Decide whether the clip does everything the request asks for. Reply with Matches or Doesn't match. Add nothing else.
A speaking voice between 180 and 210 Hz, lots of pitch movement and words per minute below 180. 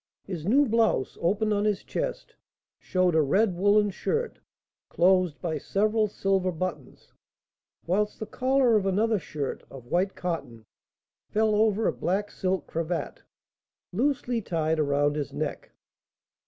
Doesn't match